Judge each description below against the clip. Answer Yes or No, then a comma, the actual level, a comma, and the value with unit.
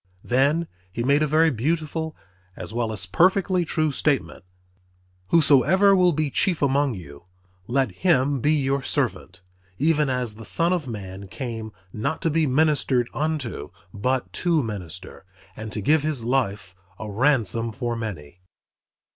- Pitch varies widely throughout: Yes, wide, 6.0 semitones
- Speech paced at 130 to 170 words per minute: Yes, average, 145 wpm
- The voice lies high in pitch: No, low, 135 Hz